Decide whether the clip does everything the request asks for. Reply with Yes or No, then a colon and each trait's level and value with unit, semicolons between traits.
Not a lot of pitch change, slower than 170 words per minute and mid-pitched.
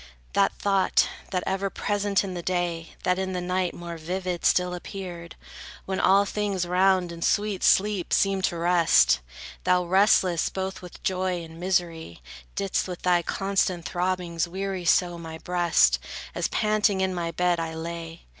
Yes: narrow, 1.9 semitones; average, 160 wpm; medium, 180 Hz